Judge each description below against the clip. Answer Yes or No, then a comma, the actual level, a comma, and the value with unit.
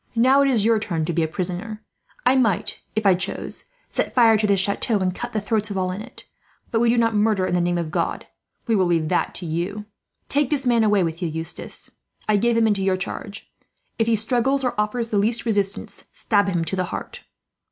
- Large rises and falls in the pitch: No, average, 3.8 semitones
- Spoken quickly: Yes, fast, 230 wpm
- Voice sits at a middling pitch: No, high, 210 Hz